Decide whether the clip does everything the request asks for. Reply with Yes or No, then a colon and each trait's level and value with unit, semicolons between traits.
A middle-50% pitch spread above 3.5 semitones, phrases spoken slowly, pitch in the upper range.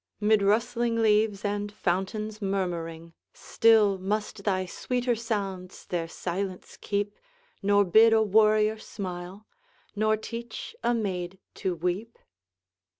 No: average, 2.7 semitones; slow, 115 wpm; high, 205 Hz